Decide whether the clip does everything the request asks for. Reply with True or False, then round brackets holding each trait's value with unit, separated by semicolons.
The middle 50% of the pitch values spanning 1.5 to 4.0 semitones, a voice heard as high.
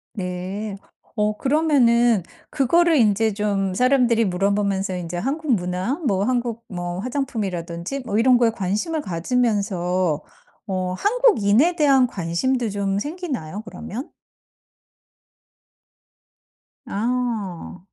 False (5.2 semitones; 210 Hz)